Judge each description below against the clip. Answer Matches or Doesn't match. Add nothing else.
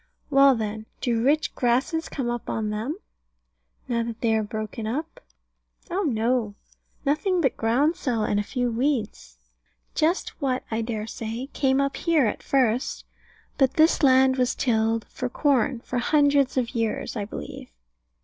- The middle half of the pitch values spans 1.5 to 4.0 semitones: Matches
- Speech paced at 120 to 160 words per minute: Matches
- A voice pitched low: Doesn't match